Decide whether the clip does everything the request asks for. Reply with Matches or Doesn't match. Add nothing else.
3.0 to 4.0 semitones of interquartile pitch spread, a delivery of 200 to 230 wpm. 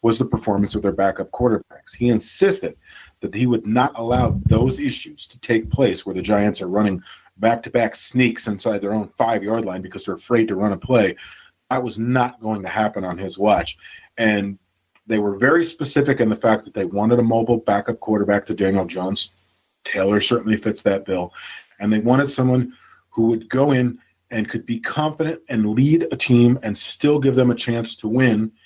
Matches